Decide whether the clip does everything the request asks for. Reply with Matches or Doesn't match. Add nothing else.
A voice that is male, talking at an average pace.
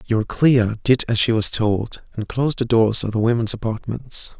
Matches